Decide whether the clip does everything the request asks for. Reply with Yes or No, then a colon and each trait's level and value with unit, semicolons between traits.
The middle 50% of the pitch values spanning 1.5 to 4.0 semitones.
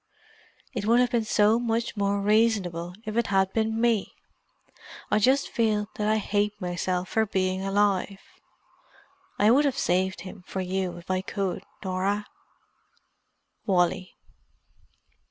Yes: average, 2.8 semitones